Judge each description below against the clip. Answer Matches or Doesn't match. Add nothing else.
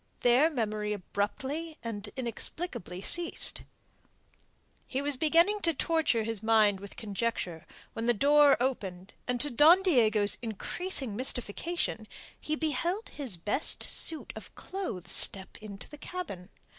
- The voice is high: Matches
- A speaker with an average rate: Doesn't match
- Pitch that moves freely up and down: Matches